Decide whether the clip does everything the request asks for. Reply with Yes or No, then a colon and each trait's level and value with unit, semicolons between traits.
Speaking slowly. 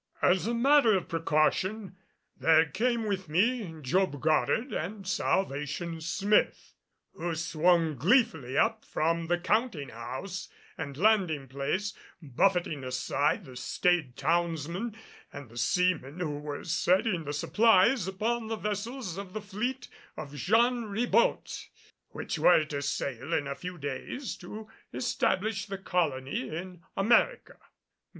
Yes: slow, 130 wpm